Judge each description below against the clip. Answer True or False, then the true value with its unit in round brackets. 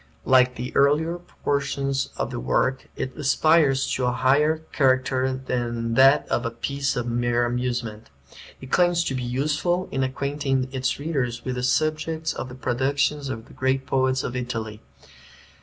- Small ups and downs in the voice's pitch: True (2.3 semitones)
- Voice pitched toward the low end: True (130 Hz)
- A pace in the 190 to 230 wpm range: False (160 wpm)